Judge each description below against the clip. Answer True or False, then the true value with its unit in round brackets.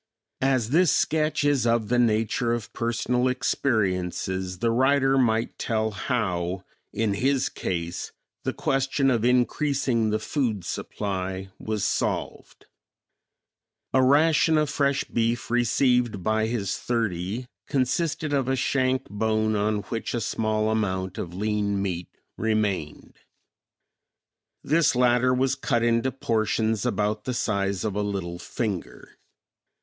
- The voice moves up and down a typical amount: True (3.9 semitones)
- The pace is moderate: False (125 wpm)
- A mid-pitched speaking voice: False (115 Hz)